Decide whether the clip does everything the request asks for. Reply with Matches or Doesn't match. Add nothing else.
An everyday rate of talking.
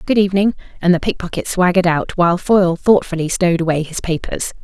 Matches